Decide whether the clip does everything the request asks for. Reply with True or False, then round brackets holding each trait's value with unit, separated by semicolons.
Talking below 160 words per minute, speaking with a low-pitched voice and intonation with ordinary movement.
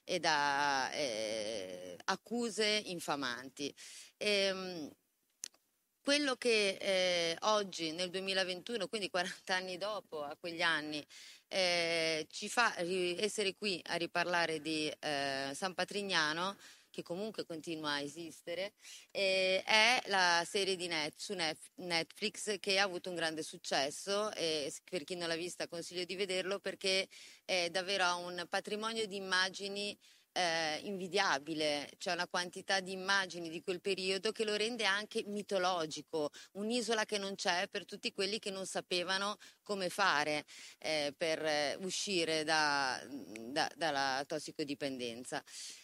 False (130 wpm; 180 Hz; 3.7 semitones)